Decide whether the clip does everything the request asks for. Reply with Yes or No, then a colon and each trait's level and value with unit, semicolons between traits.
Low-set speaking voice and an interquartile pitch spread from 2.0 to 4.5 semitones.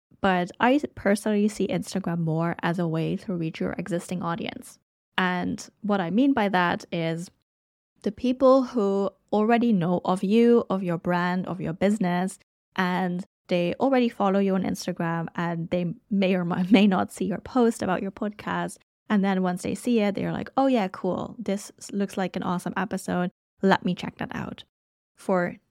No: high, 190 Hz; average, 3.1 semitones